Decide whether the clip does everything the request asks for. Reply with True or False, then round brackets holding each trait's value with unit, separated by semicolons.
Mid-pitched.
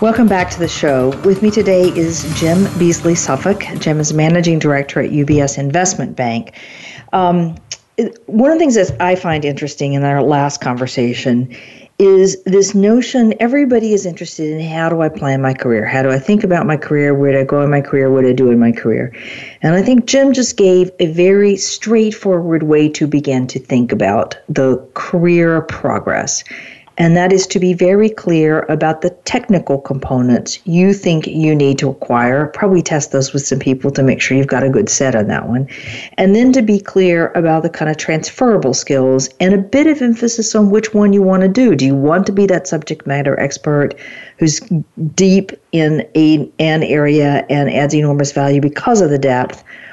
True (160 Hz)